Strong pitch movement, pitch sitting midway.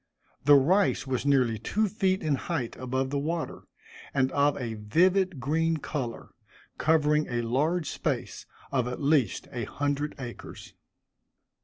No: average, 4.0 semitones; medium, 145 Hz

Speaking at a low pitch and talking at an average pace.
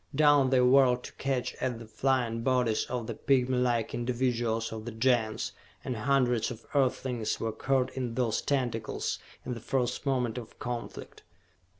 Yes: low, 125 Hz; average, 160 wpm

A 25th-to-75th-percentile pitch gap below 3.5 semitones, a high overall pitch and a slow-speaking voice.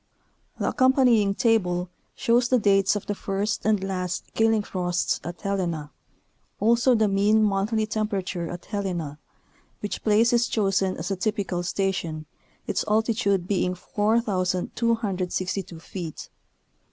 Yes: average, 3.1 semitones; high, 200 Hz; slow, 125 wpm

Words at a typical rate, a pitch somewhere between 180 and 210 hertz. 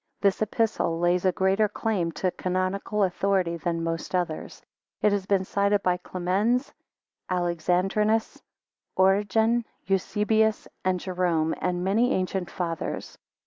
No: slow, 120 wpm; high, 190 Hz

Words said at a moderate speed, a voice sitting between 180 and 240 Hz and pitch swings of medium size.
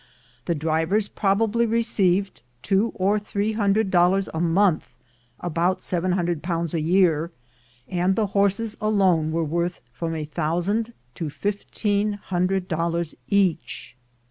No: slow, 125 wpm; medium, 185 Hz; average, 3.3 semitones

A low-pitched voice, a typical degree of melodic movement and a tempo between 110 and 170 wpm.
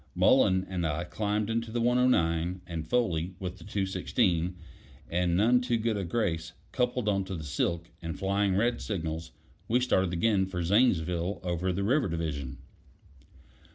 Yes: very low, 95 Hz; average, 4.4 semitones; average, 155 wpm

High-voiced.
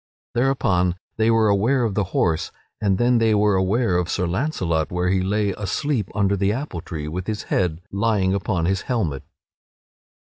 No: low, 100 Hz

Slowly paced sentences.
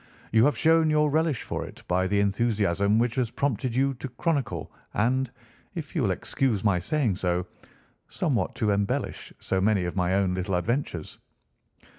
No: average, 170 wpm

